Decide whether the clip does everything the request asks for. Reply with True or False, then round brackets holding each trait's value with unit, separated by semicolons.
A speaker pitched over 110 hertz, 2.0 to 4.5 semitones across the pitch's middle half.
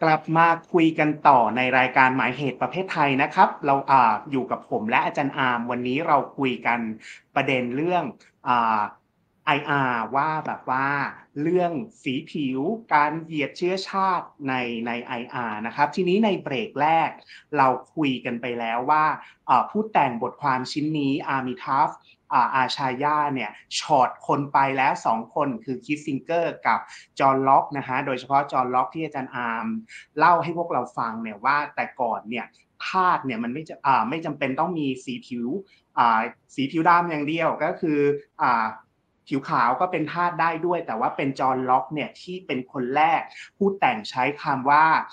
True (140 Hz; 4.1 semitones)